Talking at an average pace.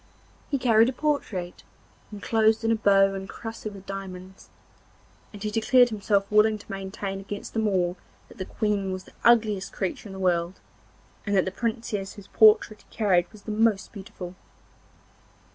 Yes: average, 165 wpm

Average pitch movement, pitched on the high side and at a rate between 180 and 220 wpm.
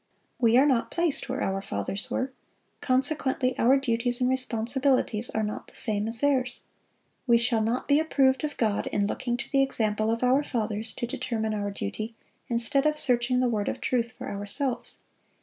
Yes: average, 3.3 semitones; high, 240 Hz; average, 185 wpm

